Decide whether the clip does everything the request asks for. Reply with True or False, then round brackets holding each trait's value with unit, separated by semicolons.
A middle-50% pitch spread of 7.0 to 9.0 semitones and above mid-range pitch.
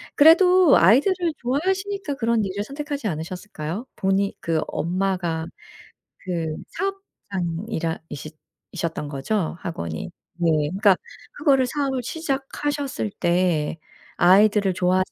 True (8.4 semitones; 200 Hz)